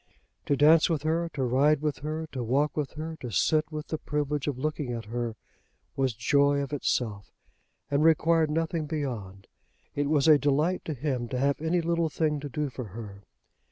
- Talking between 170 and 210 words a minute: Yes, average, 190 wpm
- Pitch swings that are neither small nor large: Yes, average, 3.3 semitones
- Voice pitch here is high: No, medium, 145 Hz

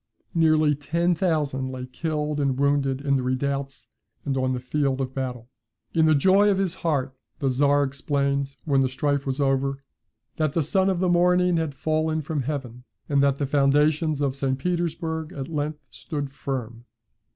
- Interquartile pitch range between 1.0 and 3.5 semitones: Yes, average, 2.8 semitones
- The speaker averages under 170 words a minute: No, average, 175 wpm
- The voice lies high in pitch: No, medium, 140 Hz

